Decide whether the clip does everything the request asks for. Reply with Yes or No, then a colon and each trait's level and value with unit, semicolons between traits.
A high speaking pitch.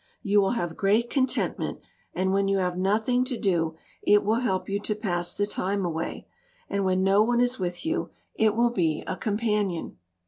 Yes: high, 200 Hz